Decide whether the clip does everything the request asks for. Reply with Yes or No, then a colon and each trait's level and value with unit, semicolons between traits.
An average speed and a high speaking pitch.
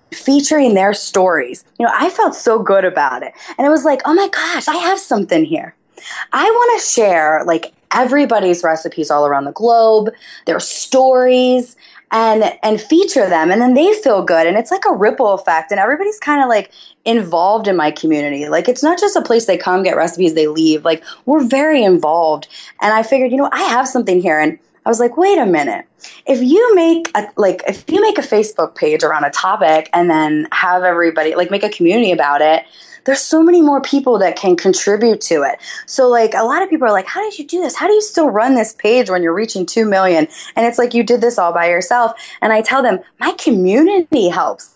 No: fast, 225 wpm; high, 230 Hz